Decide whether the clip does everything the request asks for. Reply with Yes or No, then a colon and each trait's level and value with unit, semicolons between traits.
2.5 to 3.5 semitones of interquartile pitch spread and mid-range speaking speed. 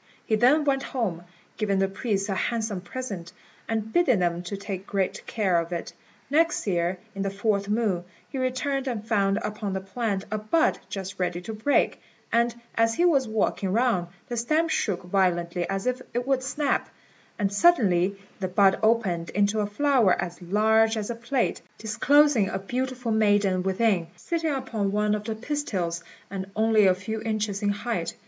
No: average, 3.9 semitones; average, 175 wpm